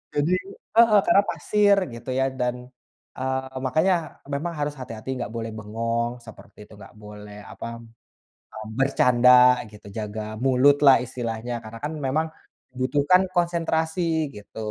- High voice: No, low, 130 Hz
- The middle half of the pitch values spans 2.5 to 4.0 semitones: No, average, 4.9 semitones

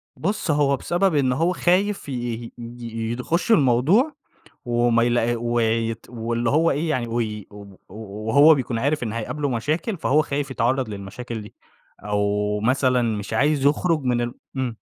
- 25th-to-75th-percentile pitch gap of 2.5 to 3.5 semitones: No, average, 4.3 semitones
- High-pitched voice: No, low, 120 Hz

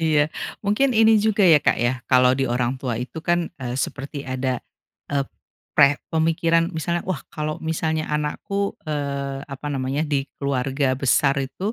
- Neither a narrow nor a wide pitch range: Yes, average, 3.5 semitones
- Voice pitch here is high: No, medium, 145 Hz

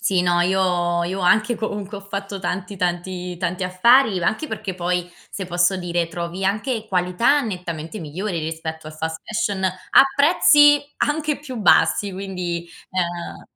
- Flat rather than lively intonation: No, average, 3.1 semitones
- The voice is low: No, medium, 185 Hz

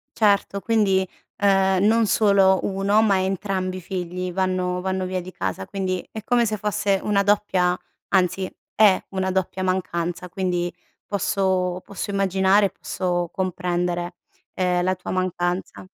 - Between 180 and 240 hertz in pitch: Yes, high, 190 Hz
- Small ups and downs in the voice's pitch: Yes, narrow, 1.6 semitones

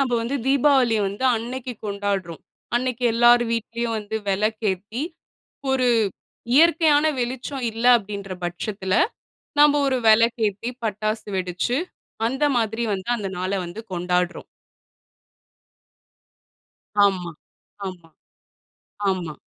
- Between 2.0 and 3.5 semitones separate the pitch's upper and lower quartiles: No, average, 4.3 semitones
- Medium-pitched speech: No, high, 220 Hz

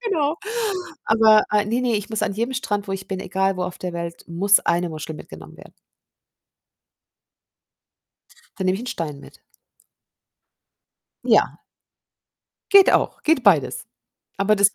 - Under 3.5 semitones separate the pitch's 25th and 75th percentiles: No, average, 3.8 semitones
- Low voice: No, high, 200 Hz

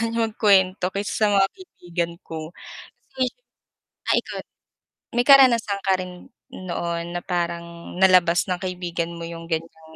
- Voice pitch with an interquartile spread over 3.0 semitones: No, average, 2.7 semitones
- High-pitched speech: No, medium, 180 Hz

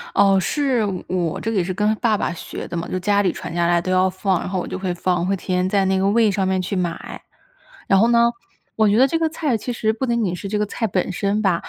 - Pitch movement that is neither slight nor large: Yes, average, 3.0 semitones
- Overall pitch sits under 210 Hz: Yes, high, 195 Hz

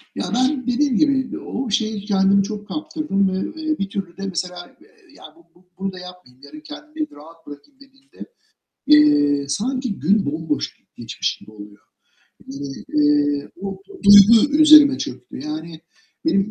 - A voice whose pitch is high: Yes, high, 200 Hz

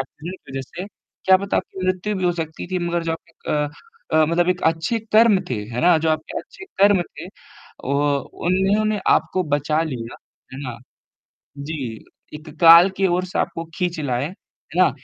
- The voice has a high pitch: No, medium, 170 Hz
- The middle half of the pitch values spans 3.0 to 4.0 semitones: Yes, average, 3.3 semitones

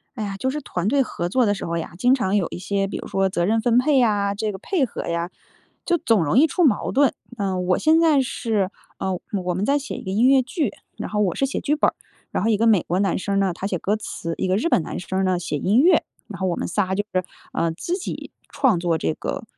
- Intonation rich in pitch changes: Yes, wide, 5.7 semitones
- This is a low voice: No, high, 205 Hz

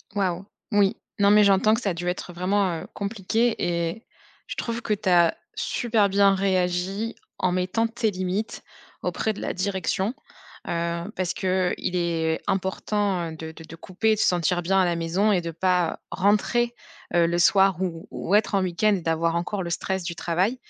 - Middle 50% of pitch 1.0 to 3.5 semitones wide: Yes, average, 2.9 semitones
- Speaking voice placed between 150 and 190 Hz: Yes, medium, 185 Hz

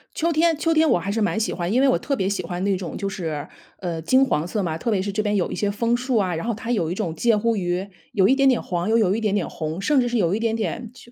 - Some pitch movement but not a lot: Yes, average, 4.9 semitones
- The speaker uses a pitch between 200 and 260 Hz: Yes, high, 210 Hz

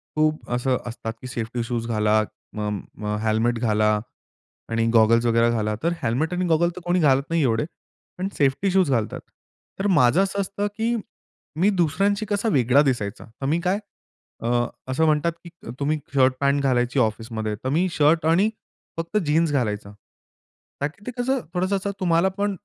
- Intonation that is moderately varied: No, wide, 7.5 semitones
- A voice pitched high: No, medium, 145 Hz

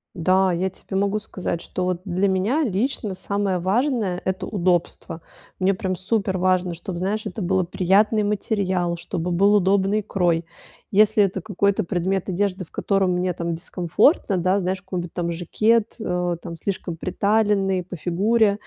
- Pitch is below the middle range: No, high, 190 Hz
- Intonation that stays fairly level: Yes, narrow, 2.3 semitones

